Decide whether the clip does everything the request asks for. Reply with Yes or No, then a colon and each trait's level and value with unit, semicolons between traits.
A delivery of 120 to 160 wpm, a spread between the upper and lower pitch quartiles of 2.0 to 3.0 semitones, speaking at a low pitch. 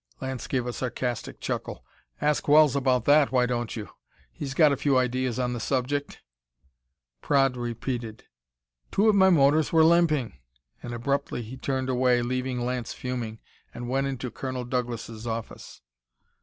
Yes: average, 155 wpm; narrow, 2.4 semitones; low, 130 Hz